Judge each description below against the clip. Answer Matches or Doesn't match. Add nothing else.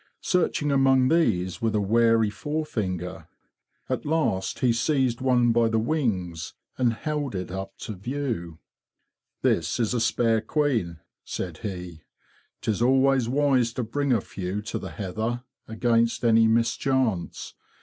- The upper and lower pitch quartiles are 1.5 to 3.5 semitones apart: Doesn't match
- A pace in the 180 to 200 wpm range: Doesn't match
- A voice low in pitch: Matches